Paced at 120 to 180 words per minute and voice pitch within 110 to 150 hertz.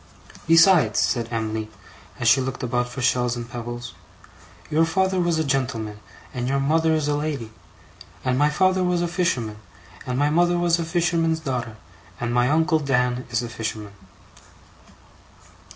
Yes: average, 160 wpm; low, 135 Hz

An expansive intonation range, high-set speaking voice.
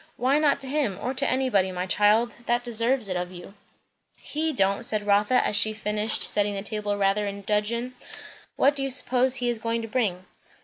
No: average, 3.9 semitones; high, 220 Hz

